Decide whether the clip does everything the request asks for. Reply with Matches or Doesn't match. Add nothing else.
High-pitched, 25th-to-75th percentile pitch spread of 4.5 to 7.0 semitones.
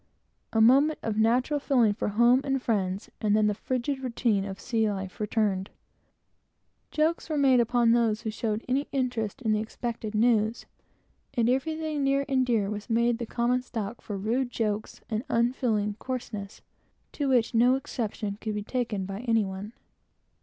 Doesn't match